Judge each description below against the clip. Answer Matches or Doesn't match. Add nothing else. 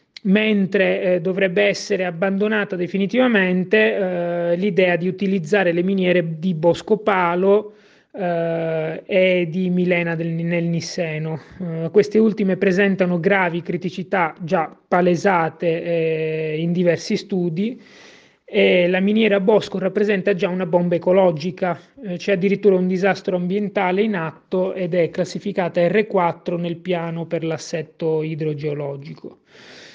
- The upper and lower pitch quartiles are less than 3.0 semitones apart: Matches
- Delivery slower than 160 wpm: Matches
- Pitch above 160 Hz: Matches